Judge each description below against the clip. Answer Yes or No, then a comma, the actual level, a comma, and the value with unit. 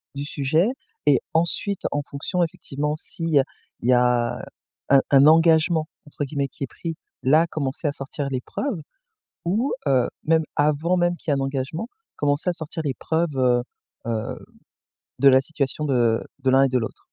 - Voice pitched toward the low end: No, medium, 145 Hz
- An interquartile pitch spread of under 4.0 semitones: Yes, average, 3.4 semitones